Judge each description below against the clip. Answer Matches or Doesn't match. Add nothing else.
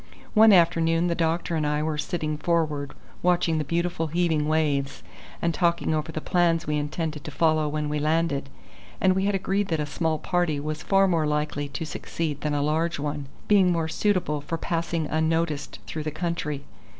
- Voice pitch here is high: Doesn't match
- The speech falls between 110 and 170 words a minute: Doesn't match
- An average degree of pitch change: Doesn't match